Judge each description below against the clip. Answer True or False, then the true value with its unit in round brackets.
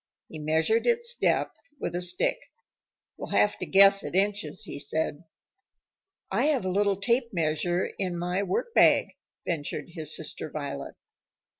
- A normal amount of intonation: True (4.5 semitones)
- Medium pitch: True (180 Hz)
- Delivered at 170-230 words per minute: False (145 wpm)